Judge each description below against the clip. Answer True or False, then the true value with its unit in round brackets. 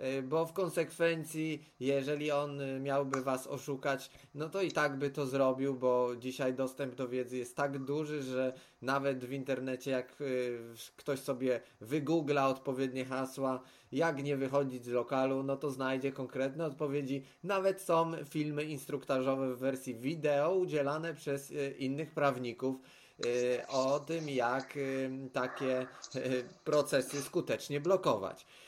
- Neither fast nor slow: True (130 wpm)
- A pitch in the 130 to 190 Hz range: True (135 Hz)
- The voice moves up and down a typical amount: False (2.1 semitones)